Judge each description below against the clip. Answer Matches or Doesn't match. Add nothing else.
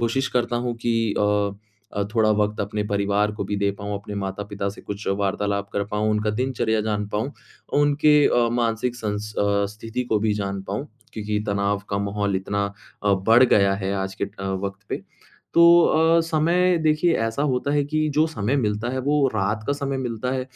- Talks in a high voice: Doesn't match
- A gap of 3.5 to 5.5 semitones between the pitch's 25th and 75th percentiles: Matches